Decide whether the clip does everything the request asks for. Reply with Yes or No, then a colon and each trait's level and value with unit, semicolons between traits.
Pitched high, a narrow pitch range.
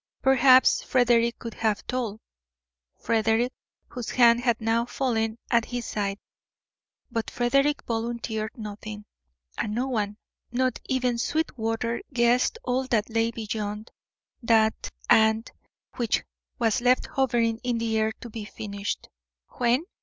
Yes: high, 230 Hz; narrow, 2.0 semitones